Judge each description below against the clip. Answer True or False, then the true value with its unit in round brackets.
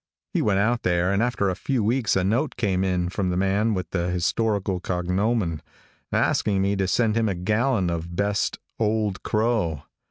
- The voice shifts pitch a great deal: False (3.4 semitones)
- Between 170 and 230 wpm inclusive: True (185 wpm)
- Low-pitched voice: True (100 Hz)